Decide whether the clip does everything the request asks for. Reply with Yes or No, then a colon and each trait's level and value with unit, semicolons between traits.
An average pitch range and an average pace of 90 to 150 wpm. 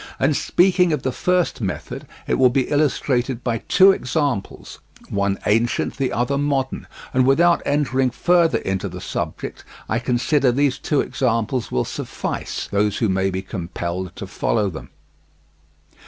No: wide, 5.8 semitones; average, 140 wpm